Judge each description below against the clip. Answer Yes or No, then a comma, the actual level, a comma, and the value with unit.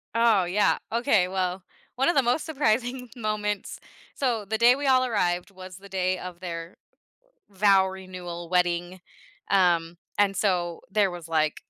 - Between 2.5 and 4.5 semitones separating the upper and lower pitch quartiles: Yes, average, 3.9 semitones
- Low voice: No, high, 190 Hz